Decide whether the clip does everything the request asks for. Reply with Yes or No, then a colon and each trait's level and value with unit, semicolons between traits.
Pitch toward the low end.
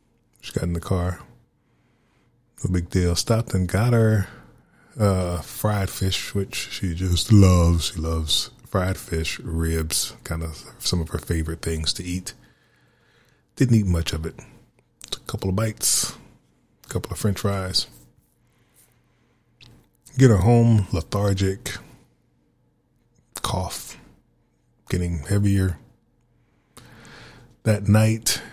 Yes: very low, 95 Hz